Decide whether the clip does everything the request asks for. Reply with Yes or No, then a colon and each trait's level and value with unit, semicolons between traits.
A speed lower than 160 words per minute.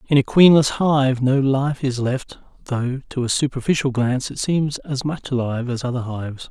No: average, 195 wpm